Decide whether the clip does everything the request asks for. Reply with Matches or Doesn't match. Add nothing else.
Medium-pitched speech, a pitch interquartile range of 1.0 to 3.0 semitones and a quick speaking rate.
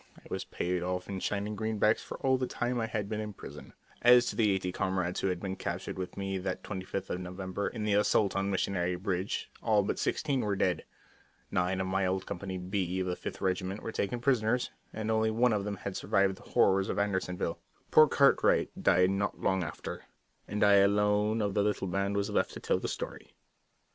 Doesn't match